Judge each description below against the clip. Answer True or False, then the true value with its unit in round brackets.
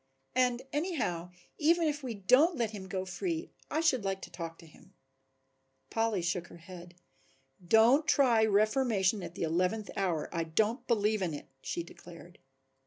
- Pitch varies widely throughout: True (6.2 semitones)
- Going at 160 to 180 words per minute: True (165 wpm)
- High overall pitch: True (210 Hz)